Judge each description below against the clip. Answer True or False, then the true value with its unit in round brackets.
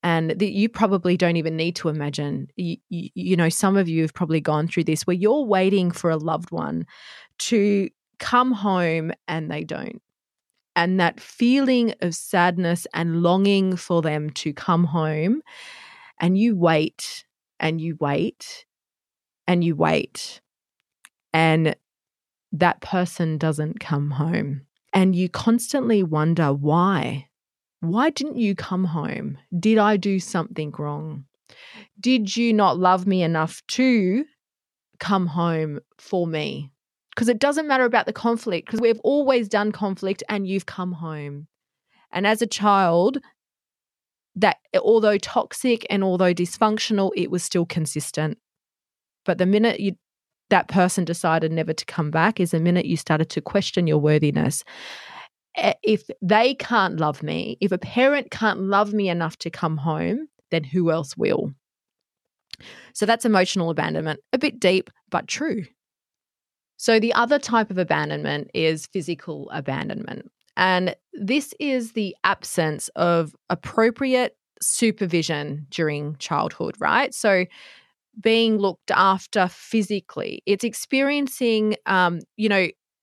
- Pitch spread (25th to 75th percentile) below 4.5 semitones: False (5.1 semitones)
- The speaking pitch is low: False (185 Hz)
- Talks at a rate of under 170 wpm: True (140 wpm)